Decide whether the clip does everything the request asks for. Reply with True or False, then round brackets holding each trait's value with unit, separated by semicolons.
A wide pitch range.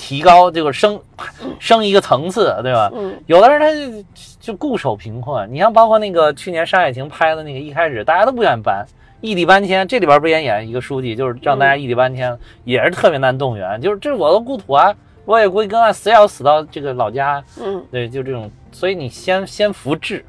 True (7.5 semitones)